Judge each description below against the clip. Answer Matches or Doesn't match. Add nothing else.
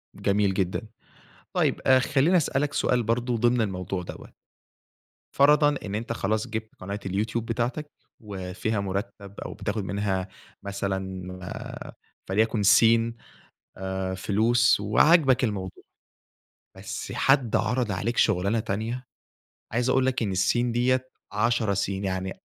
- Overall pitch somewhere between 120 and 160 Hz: Doesn't match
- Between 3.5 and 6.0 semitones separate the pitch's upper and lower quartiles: Matches